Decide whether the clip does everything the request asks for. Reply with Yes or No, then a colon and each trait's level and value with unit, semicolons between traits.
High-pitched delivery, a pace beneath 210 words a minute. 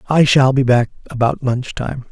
No: low, 130 Hz; average, 200 wpm